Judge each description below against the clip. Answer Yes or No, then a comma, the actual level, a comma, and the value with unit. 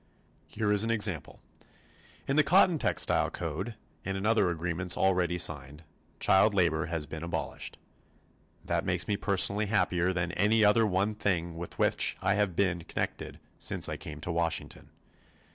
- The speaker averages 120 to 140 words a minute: No, average, 160 wpm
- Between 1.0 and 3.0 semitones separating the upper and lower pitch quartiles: No, average, 3.6 semitones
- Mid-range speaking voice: No, very low, 95 Hz